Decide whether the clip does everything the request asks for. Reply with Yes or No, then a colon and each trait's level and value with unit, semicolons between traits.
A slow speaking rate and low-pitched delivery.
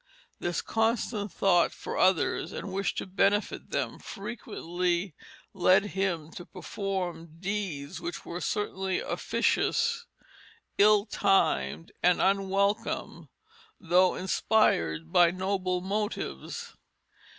No: slow, 100 wpm; high, 190 Hz